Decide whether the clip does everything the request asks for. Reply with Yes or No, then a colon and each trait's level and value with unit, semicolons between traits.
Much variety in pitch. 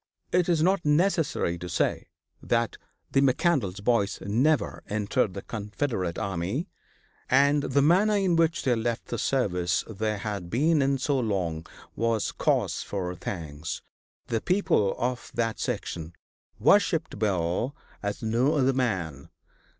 Yes: wide, 6.6 semitones